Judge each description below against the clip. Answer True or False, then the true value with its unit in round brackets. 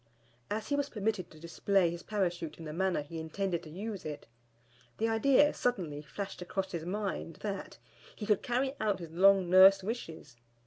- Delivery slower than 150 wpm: False (180 wpm)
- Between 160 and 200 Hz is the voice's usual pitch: True (190 Hz)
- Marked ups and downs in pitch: False (4.1 semitones)